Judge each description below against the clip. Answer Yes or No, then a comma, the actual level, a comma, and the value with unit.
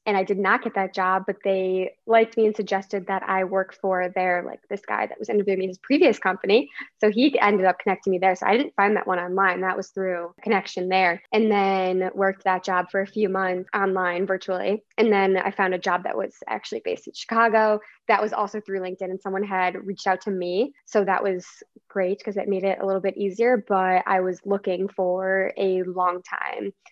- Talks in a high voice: Yes, high, 195 Hz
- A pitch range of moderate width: No, narrow, 1.6 semitones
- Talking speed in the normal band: No, fast, 225 wpm